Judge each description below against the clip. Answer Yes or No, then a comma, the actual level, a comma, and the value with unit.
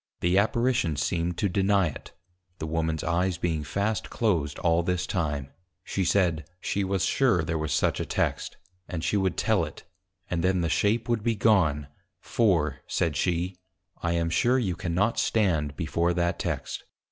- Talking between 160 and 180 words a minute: Yes, average, 170 wpm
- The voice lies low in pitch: Yes, very low, 85 Hz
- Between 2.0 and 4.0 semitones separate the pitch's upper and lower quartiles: Yes, average, 3.6 semitones